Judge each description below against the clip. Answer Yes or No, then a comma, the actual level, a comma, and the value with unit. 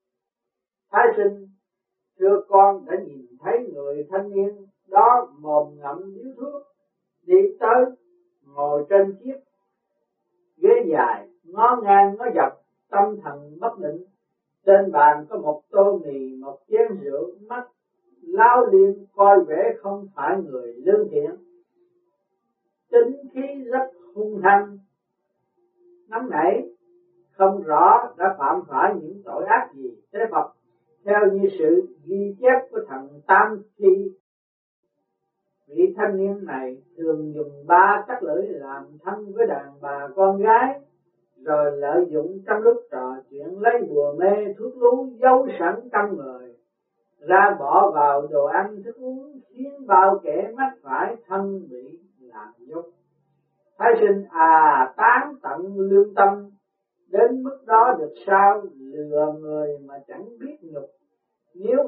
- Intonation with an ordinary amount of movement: No, wide, 8.6 semitones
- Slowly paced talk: Yes, slow, 140 wpm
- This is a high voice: Yes, high, 200 Hz